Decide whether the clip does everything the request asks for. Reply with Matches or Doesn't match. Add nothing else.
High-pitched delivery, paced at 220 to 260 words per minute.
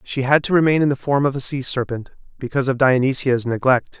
Doesn't match